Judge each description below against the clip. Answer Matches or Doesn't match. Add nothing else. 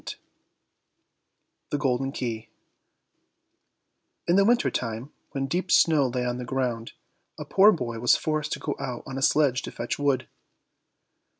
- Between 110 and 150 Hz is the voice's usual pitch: Matches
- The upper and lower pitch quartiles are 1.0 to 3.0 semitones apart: Doesn't match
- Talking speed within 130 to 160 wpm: Matches